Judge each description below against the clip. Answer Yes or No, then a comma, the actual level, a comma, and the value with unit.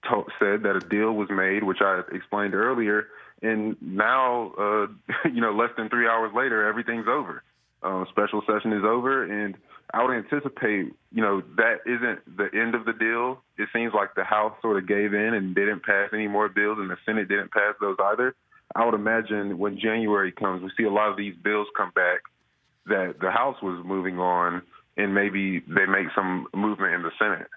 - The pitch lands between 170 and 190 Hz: No, low, 105 Hz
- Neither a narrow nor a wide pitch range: No, narrow, 2.2 semitones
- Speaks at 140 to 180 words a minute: No, average, 200 wpm